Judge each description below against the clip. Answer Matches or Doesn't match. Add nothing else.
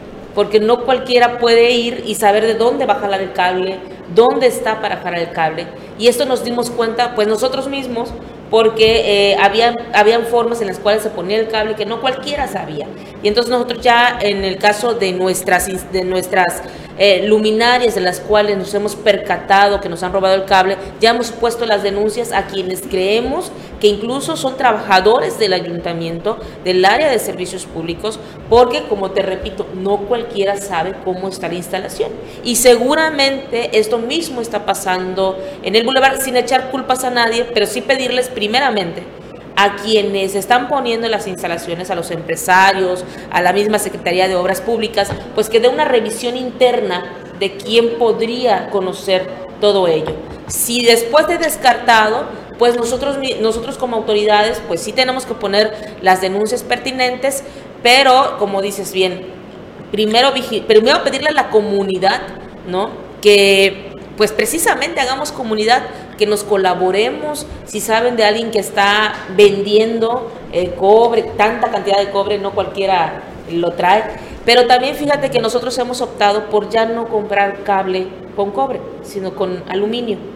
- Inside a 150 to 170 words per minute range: Matches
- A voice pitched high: Matches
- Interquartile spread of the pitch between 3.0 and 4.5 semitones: Matches